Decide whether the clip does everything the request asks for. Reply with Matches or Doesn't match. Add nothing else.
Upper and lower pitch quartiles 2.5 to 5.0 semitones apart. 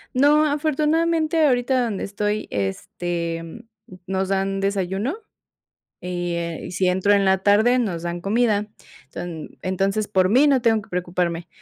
Doesn't match